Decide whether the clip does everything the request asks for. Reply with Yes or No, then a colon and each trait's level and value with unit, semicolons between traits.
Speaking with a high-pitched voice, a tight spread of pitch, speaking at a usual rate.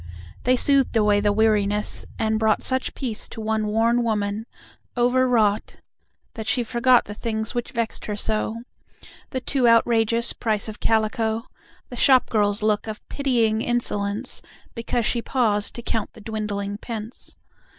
Yes: high, 220 Hz; narrow, 2.1 semitones; average, 150 wpm